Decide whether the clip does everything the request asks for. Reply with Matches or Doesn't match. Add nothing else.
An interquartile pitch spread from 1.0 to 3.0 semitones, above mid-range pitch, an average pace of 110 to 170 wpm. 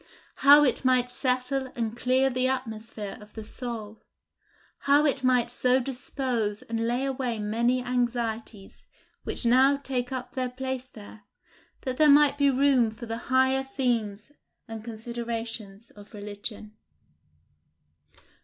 Matches